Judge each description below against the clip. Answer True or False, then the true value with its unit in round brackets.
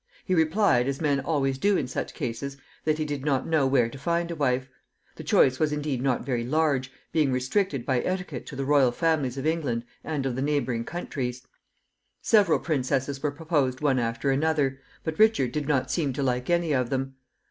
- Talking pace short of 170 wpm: False (200 wpm)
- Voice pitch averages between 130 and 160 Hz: True (140 Hz)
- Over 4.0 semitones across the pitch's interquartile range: False (3.3 semitones)